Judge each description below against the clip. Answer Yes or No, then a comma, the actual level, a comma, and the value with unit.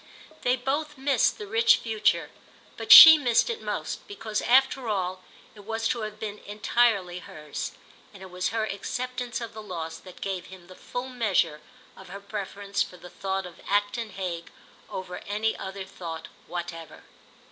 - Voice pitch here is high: Yes, high, 205 Hz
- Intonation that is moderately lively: Yes, average, 4.0 semitones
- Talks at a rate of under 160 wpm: No, average, 170 wpm